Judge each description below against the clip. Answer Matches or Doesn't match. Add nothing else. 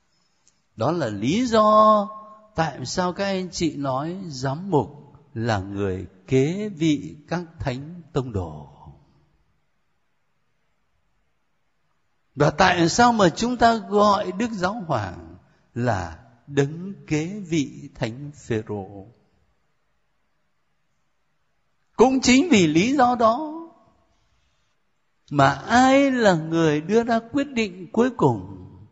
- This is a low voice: Doesn't match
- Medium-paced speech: Doesn't match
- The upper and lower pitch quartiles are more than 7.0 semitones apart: Matches